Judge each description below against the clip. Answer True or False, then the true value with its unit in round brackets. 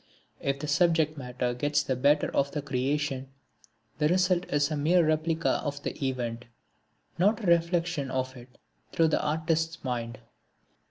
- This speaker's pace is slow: False (155 wpm)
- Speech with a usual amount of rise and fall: True (3.7 semitones)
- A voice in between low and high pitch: True (145 Hz)